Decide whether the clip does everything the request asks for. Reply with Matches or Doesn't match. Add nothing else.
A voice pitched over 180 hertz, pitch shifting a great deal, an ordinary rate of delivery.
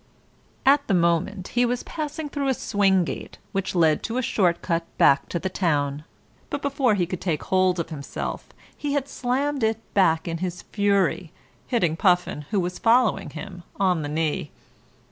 Matches